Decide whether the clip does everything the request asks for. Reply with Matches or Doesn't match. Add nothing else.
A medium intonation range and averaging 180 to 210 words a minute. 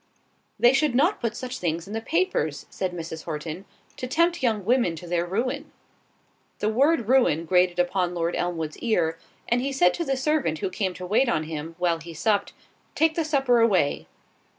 Doesn't match